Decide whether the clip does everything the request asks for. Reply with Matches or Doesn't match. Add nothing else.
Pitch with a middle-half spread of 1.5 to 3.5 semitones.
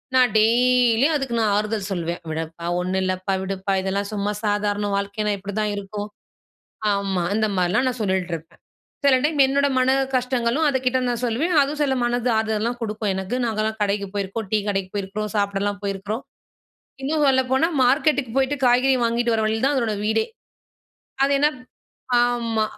Doesn't match